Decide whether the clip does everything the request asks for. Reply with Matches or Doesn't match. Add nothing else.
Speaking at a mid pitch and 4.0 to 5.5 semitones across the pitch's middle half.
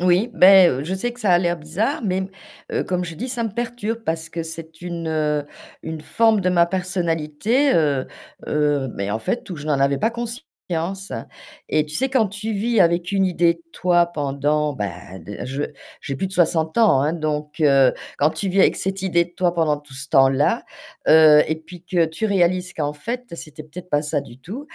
Matches